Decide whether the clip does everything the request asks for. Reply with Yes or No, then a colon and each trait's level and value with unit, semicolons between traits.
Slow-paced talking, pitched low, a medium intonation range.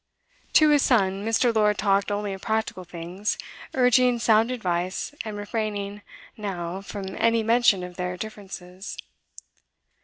No: slow, 130 wpm; high, 205 Hz; average, 3.0 semitones